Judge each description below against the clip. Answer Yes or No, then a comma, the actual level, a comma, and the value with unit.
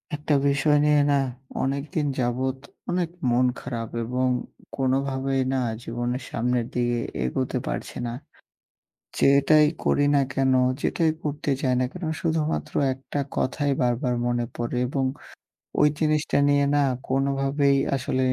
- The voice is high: No, low, 135 Hz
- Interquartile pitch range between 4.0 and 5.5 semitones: No, narrow, 2.5 semitones